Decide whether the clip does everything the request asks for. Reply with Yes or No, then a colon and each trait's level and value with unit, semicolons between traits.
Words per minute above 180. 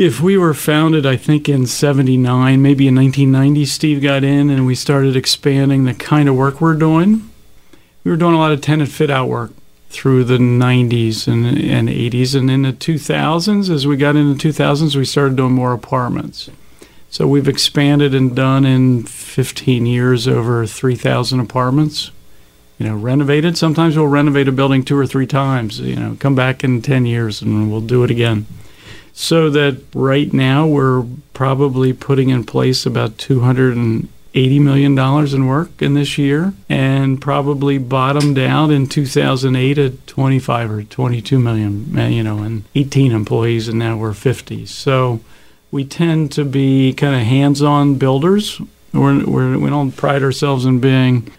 No: average, 165 wpm